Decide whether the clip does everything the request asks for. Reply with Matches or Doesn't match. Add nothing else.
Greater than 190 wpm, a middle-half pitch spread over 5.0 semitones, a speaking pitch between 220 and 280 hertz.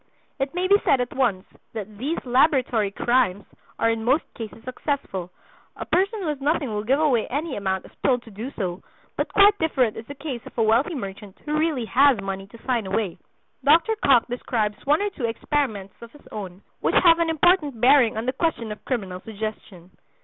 Matches